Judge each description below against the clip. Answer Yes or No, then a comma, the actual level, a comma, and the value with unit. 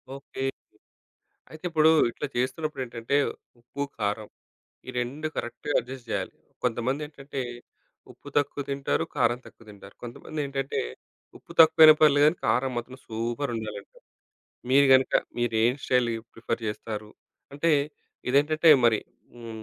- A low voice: Yes, low, 130 Hz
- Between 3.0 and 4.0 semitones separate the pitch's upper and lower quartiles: Yes, average, 3.6 semitones